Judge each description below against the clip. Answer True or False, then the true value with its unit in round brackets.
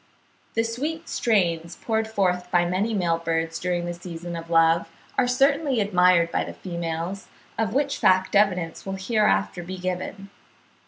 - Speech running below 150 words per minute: False (155 wpm)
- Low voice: False (185 Hz)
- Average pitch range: True (4.3 semitones)